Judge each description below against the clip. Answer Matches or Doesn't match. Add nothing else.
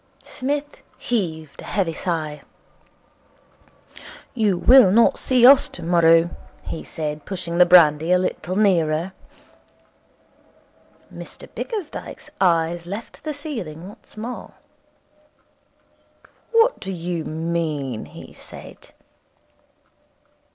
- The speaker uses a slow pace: Matches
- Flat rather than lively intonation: Doesn't match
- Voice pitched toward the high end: Doesn't match